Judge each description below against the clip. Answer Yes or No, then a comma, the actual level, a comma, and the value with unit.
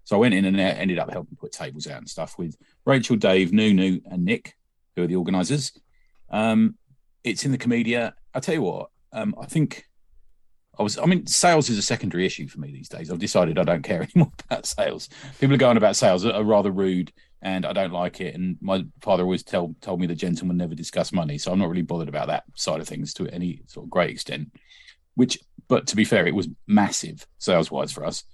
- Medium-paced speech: No, fast, 235 wpm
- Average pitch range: No, wide, 6.4 semitones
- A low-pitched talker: Yes, very low, 95 Hz